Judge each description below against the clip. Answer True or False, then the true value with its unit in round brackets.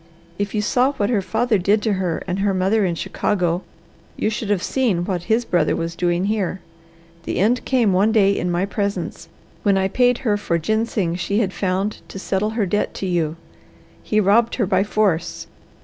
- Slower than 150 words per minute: False (195 wpm)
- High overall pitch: True (200 Hz)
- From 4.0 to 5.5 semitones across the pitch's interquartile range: False (3.0 semitones)